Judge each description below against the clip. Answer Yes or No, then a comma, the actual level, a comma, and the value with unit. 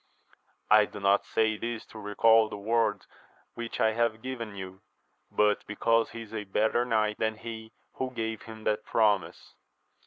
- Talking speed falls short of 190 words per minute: Yes, average, 165 wpm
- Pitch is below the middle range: Yes, low, 110 Hz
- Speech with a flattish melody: Yes, narrow, 1.5 semitones